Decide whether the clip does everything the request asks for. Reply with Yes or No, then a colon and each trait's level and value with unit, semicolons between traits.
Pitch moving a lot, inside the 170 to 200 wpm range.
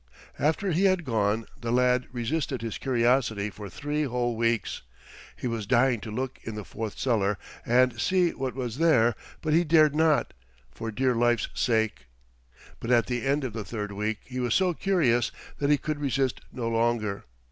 No: average, 4.0 semitones; average, 180 wpm